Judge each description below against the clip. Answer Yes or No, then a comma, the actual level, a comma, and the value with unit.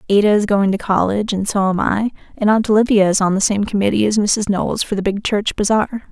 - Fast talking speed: Yes, fast, 245 wpm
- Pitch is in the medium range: No, high, 205 Hz